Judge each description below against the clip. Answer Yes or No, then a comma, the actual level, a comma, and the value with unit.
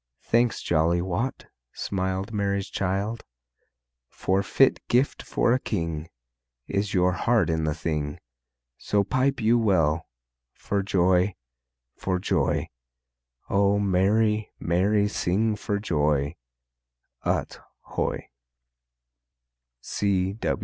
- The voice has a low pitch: Yes, low, 100 Hz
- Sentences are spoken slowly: Yes, slow, 100 wpm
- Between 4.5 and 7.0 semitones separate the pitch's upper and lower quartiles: No, average, 3.5 semitones